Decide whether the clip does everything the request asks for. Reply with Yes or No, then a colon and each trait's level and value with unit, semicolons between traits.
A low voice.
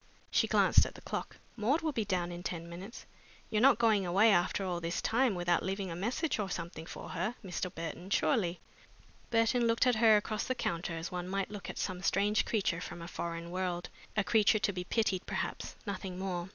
No: high, 190 Hz